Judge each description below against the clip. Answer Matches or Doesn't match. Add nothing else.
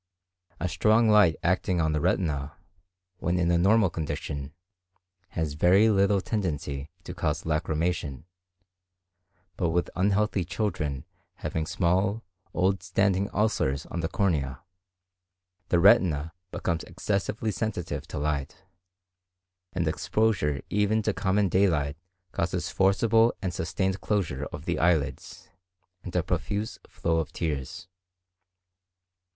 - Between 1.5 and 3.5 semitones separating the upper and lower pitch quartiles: Doesn't match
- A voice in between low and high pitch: Doesn't match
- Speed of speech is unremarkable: Doesn't match